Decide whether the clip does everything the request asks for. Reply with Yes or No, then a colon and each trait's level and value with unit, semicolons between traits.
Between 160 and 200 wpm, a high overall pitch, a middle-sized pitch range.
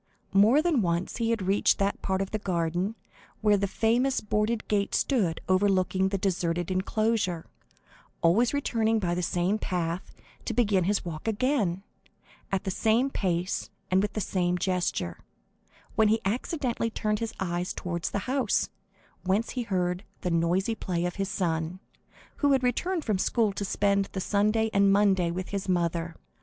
Yes: average, 165 wpm; high, 195 Hz; average, 3.7 semitones